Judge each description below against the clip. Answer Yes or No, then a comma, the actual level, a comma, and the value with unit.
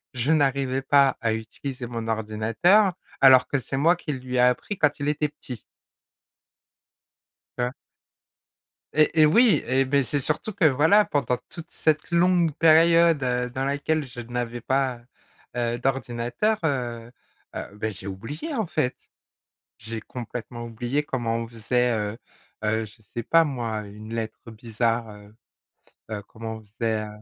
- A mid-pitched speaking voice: No, low, 125 Hz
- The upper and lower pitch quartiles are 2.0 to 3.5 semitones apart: No, average, 4.6 semitones